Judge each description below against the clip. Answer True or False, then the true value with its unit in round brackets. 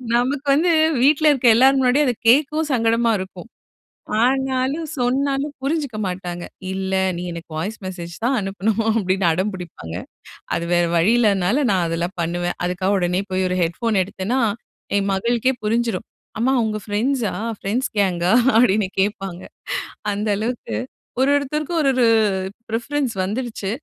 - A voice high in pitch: True (220 Hz)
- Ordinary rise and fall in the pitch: False (5.8 semitones)